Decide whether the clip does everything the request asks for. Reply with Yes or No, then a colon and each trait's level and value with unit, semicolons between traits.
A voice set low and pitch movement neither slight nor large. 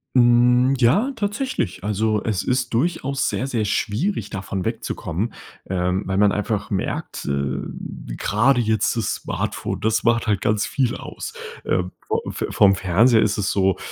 Yes: low, 110 Hz; average, 4.2 semitones